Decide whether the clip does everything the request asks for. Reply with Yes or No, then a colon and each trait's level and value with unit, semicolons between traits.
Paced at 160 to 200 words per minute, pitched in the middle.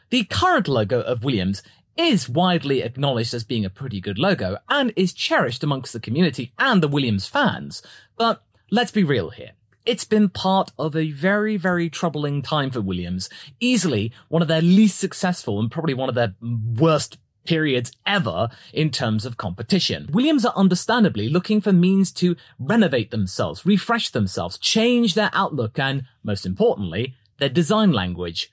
Yes: average, 165 wpm; medium, 155 Hz